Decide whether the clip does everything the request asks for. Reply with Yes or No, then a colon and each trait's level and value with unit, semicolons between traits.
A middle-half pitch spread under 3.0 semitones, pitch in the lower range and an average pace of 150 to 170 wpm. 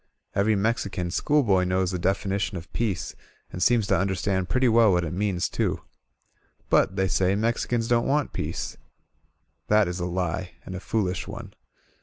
No: average, 3.5 semitones; low, 100 Hz; average, 165 wpm